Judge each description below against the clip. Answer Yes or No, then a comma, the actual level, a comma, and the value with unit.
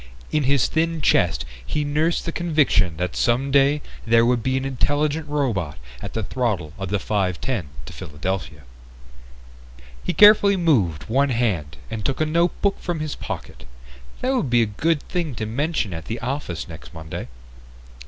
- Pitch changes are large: Yes, wide, 8.2 semitones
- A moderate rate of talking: Yes, average, 165 wpm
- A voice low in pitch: Yes, low, 125 Hz